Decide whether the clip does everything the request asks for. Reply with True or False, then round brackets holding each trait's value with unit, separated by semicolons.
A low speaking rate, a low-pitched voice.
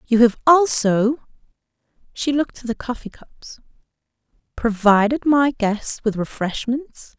False (100 wpm; 245 Hz)